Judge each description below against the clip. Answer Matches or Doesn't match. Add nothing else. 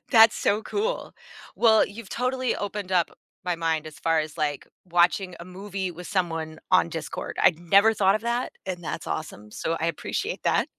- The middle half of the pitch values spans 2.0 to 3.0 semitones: Doesn't match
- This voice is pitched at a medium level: Matches